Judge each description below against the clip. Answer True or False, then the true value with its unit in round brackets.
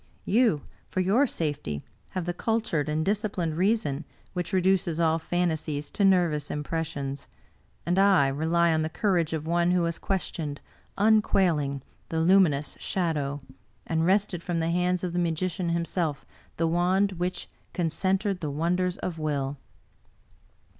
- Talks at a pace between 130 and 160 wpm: True (150 wpm)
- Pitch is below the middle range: False (170 Hz)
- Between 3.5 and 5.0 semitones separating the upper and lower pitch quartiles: False (3.1 semitones)